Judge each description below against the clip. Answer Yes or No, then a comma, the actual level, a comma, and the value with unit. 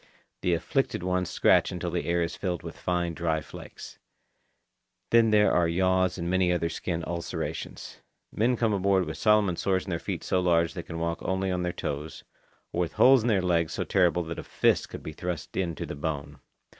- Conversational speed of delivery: No, fast, 210 wpm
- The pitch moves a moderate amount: No, narrow, 2.0 semitones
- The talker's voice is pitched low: Yes, very low, 90 Hz